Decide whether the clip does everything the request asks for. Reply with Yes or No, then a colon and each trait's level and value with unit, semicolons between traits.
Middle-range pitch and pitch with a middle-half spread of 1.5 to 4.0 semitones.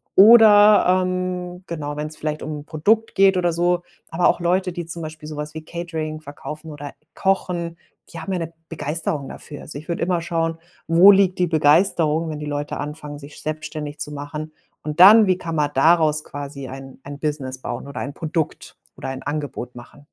Yes: medium, 155 Hz; average, 3.0 semitones